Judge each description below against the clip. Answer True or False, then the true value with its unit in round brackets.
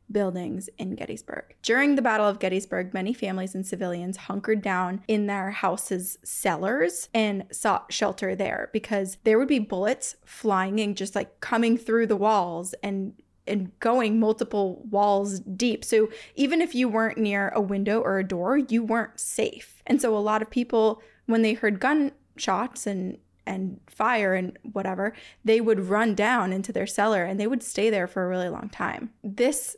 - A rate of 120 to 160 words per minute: False (175 wpm)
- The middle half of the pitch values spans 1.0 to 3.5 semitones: True (3.0 semitones)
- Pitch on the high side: True (215 Hz)